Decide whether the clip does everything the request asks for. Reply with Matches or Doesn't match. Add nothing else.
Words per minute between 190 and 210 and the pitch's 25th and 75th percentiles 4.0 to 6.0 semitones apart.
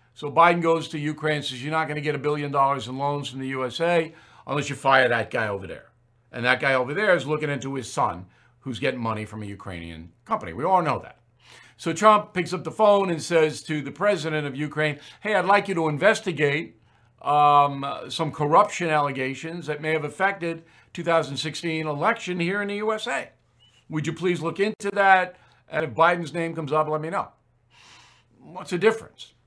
Matches